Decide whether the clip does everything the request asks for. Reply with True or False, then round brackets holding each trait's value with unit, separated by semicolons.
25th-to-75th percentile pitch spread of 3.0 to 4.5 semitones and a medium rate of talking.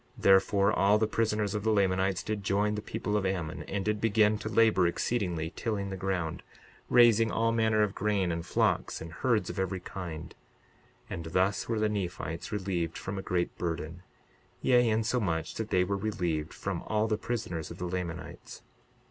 True (3.3 semitones; 180 wpm)